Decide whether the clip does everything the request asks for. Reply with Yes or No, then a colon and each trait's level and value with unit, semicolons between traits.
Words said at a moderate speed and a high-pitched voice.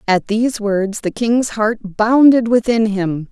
Yes: average, 165 wpm; high, 220 Hz